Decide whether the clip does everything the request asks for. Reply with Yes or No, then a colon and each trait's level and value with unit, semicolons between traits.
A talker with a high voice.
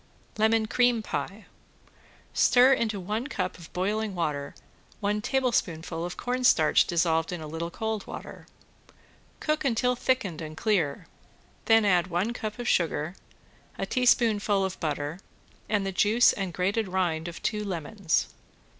Yes: high, 200 Hz